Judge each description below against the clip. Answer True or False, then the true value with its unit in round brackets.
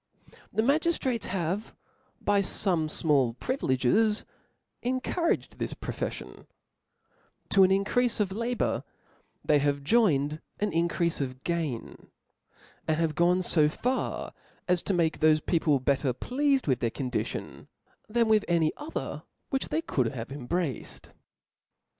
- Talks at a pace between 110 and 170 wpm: True (135 wpm)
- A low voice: False (170 Hz)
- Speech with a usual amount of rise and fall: False (6.9 semitones)